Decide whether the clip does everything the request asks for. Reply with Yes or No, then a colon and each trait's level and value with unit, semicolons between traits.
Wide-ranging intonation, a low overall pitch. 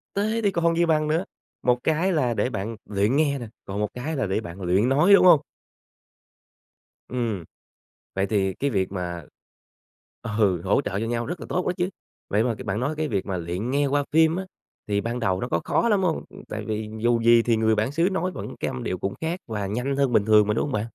Yes: wide, 7.2 semitones; low, 120 Hz